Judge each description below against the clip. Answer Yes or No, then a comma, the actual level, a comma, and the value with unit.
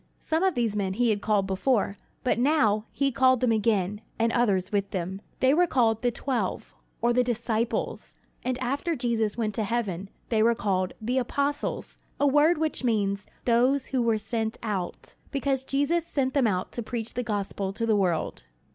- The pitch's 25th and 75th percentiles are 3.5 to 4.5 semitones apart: Yes, average, 3.9 semitones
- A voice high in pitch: Yes, high, 230 Hz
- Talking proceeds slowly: No, average, 185 wpm